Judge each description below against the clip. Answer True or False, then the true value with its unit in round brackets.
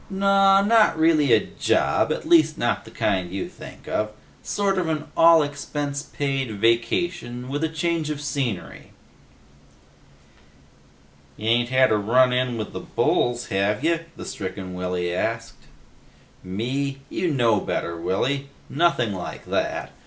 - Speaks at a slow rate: False (145 wpm)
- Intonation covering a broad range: True (6.6 semitones)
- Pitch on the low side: True (130 Hz)